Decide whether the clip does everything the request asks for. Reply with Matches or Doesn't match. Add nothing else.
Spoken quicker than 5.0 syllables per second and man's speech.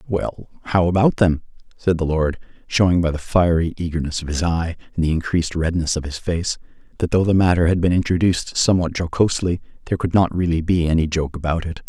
Matches